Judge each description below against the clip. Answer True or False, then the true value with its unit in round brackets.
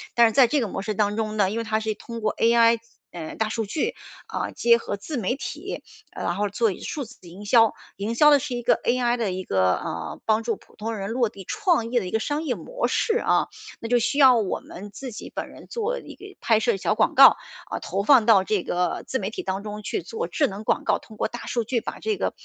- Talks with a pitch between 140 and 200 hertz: False (225 Hz)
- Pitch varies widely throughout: False (3.2 semitones)